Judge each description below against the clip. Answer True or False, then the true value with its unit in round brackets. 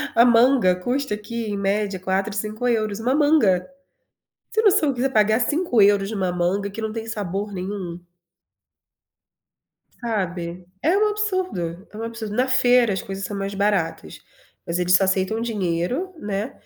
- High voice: True (210 Hz)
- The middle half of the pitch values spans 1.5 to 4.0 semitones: False (4.4 semitones)